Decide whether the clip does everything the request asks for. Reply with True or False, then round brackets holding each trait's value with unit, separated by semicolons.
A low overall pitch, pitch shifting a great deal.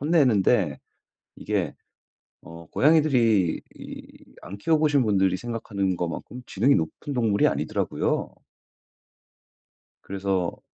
True (105 Hz; 6.4 semitones)